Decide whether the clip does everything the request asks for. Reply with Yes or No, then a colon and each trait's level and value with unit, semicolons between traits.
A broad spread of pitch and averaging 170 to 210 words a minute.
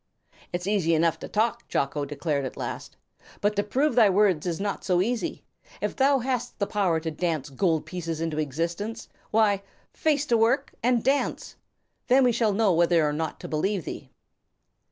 Yes: wide, 5.8 semitones; average, 180 wpm